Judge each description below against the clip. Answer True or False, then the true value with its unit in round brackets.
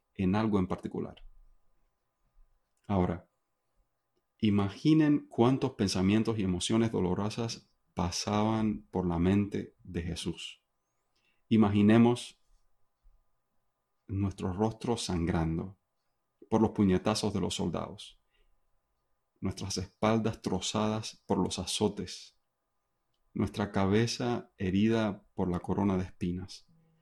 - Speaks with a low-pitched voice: True (105 Hz)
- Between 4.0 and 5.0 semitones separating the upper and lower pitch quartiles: False (3.2 semitones)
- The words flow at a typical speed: False (90 wpm)